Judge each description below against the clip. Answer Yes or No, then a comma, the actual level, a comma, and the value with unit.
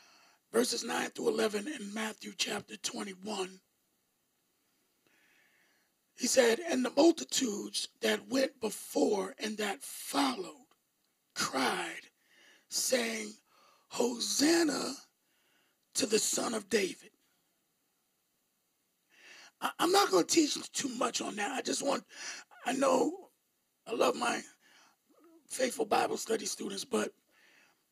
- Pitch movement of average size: No, wide, 6.5 semitones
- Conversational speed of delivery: No, slow, 105 wpm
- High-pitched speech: Yes, very high, 265 Hz